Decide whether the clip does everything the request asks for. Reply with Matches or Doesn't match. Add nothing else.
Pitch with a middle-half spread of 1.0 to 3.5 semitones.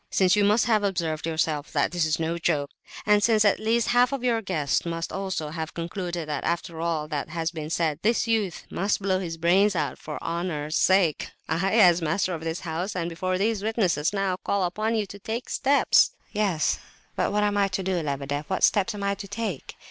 Doesn't match